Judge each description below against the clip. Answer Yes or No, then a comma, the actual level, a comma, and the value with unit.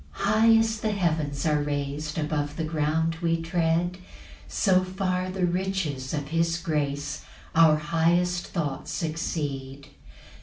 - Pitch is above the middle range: No, medium, 165 Hz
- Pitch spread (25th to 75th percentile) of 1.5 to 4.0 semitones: Yes, average, 3.4 semitones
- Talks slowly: Yes, slow, 130 wpm